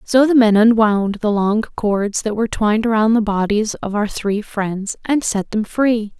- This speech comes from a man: No, female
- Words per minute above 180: Yes, fast, 205 wpm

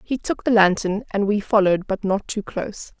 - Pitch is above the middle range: Yes, high, 205 Hz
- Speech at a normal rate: No, fast, 220 wpm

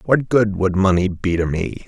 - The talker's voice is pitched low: Yes, very low, 95 Hz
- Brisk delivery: Yes, fast, 225 wpm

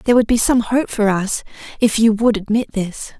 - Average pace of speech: No, fast, 225 wpm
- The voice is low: No, high, 220 Hz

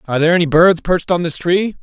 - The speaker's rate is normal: No, fast, 265 wpm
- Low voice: No, medium, 170 Hz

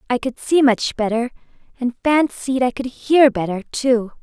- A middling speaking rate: Yes, average, 170 wpm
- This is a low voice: No, very high, 250 Hz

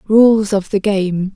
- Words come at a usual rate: Yes, average, 175 wpm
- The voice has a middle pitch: No, high, 200 Hz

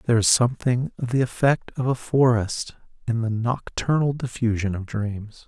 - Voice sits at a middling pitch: No, low, 120 Hz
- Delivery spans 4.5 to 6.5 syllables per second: Yes, 4.9 syllables/s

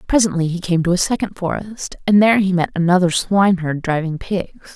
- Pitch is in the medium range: Yes, medium, 180 Hz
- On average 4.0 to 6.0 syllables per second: Yes, 5.6 syllables/s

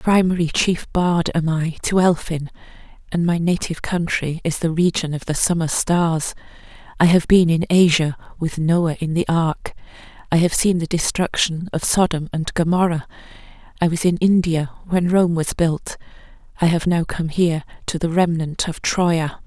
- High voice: No, medium, 170 Hz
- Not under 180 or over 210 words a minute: No, average, 170 wpm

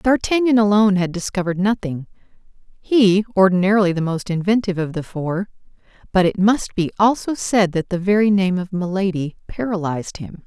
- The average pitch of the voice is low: No, high, 195 Hz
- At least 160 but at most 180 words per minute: No, average, 150 wpm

